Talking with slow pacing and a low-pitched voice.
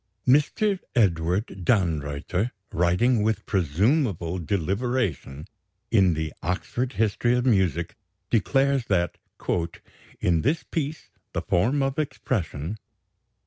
Yes: slow, 100 wpm; low, 100 Hz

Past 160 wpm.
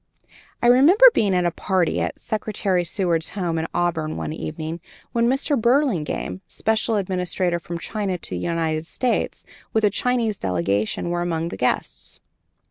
No: average, 155 wpm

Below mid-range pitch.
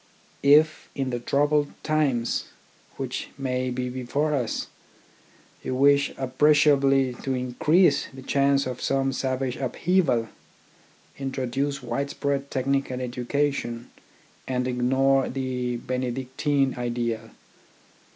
Yes: low, 130 Hz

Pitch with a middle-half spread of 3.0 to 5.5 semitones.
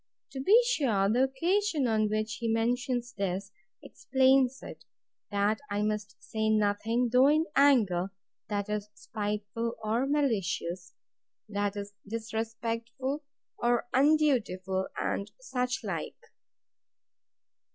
Yes: average, 4.3 semitones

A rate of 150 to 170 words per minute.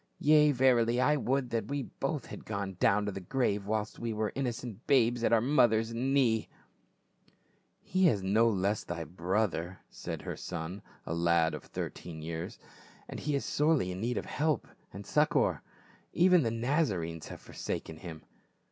No: average, 180 wpm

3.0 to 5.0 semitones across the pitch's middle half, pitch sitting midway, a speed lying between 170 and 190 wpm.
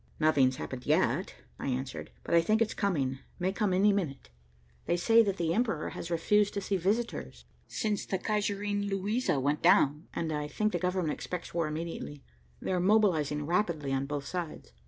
No: wide, 5.4 semitones; medium, 175 Hz; average, 175 wpm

